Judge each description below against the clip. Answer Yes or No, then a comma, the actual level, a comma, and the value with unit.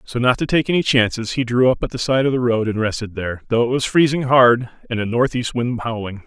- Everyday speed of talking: No, fast, 270 wpm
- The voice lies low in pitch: Yes, low, 120 Hz